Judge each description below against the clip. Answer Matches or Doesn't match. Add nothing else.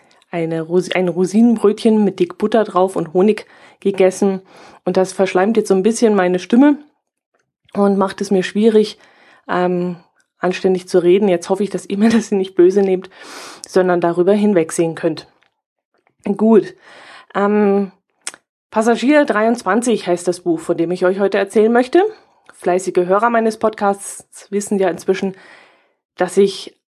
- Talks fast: Doesn't match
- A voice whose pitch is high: Matches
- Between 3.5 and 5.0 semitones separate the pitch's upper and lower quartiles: Doesn't match